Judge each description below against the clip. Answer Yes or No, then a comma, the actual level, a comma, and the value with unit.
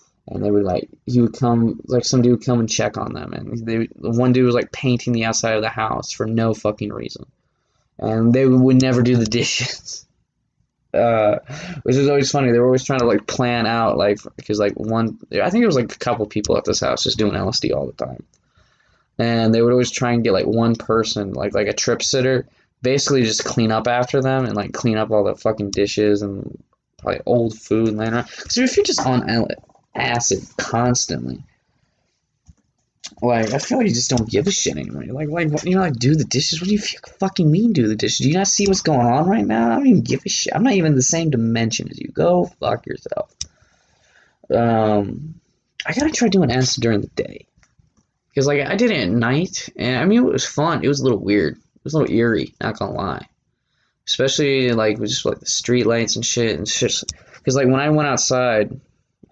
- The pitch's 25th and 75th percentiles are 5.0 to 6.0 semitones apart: No, average, 3.4 semitones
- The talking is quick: Yes, fast, 225 wpm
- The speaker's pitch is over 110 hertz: Yes, low, 120 Hz